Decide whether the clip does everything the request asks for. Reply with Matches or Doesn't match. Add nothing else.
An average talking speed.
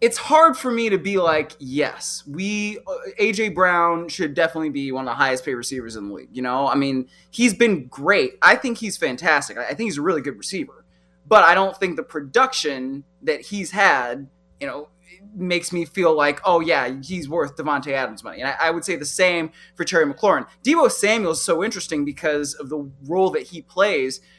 Doesn't match